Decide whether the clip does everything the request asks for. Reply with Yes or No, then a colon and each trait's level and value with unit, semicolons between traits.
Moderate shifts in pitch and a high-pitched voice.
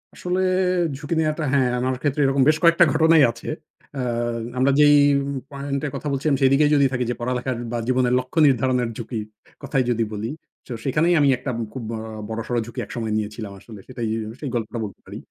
No: average, 3.7 semitones; low, 130 Hz